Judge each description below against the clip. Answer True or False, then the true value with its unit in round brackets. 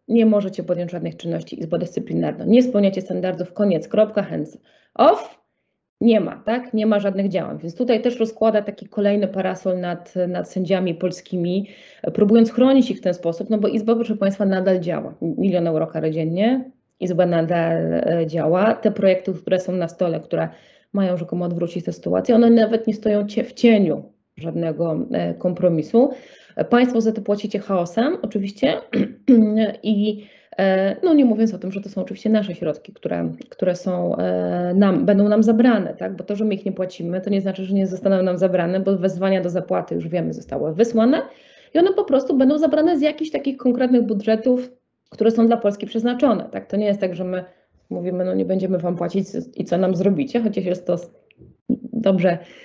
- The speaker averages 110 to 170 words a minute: False (180 wpm)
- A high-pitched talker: True (195 Hz)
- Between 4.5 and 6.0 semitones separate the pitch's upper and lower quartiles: False (3.8 semitones)